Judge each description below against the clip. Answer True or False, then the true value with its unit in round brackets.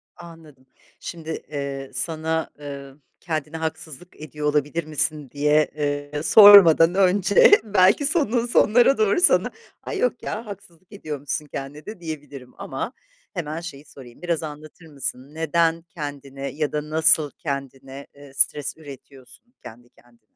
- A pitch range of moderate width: True (3.4 semitones)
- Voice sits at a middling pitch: True (155 Hz)